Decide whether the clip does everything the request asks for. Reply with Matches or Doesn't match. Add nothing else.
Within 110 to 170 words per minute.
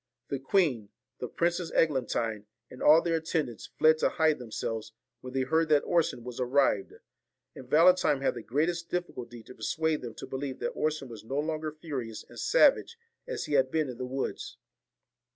Doesn't match